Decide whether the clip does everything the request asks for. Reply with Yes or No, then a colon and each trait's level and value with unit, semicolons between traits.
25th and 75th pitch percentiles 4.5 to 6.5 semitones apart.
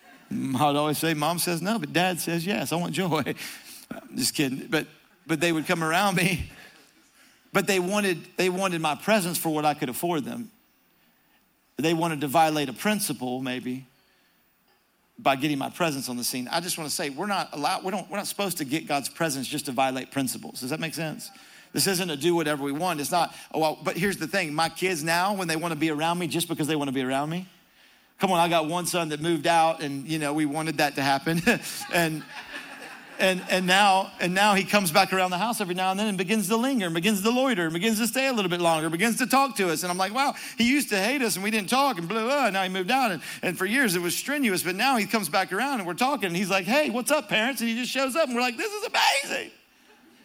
Yes: average, 5.0 semitones